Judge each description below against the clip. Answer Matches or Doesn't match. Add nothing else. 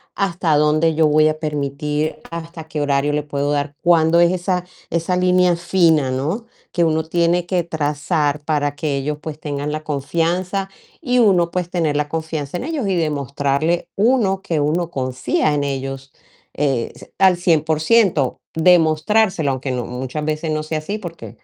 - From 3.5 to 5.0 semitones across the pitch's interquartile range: Doesn't match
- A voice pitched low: Doesn't match